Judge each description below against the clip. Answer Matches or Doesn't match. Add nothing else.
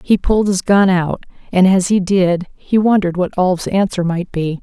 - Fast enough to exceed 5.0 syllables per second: Doesn't match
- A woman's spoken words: Matches